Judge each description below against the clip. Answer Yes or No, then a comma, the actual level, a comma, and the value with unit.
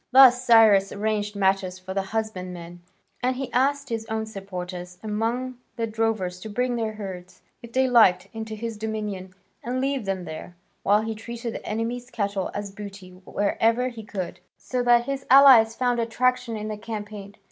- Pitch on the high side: Yes, high, 220 Hz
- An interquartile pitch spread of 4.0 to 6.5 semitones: No, average, 3.4 semitones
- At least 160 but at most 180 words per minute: Yes, average, 170 wpm